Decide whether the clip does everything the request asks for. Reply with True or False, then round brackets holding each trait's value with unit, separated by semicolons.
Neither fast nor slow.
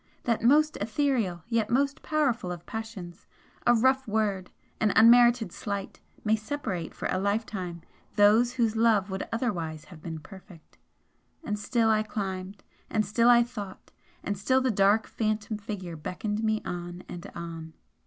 True (155 wpm)